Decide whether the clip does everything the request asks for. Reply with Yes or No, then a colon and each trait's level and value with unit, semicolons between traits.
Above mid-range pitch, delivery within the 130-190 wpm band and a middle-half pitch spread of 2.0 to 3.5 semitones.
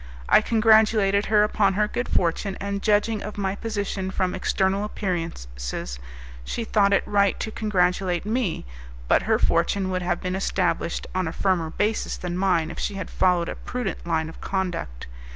Yes: high, 195 Hz; average, 170 wpm; average, 2.8 semitones